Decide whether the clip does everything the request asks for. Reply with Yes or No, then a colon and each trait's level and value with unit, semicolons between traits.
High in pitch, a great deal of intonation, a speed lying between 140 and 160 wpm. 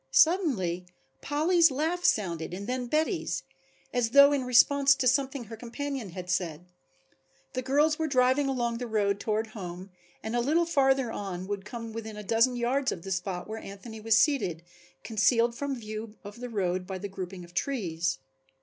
No: high, 230 Hz; wide, 5.7 semitones; average, 175 wpm